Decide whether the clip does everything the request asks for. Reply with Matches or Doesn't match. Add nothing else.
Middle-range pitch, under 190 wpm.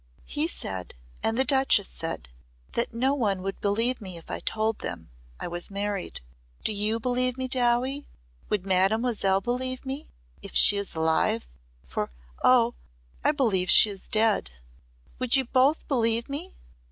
Doesn't match